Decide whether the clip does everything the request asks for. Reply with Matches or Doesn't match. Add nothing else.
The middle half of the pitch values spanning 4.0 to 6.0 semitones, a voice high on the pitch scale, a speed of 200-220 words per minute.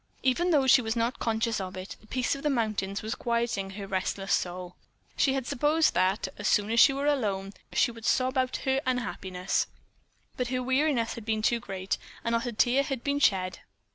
Matches